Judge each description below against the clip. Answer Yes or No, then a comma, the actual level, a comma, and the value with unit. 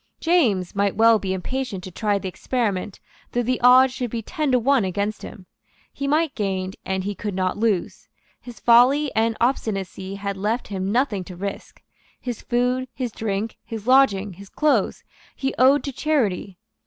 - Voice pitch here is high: Yes, high, 220 Hz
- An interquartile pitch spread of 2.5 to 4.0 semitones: No, average, 4.6 semitones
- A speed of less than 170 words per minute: No, average, 175 wpm